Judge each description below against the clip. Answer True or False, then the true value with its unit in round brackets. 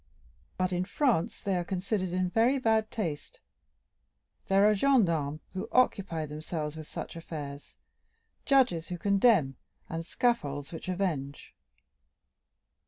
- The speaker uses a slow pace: True (120 wpm)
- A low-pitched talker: False (185 Hz)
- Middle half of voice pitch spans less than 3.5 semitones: False (5.4 semitones)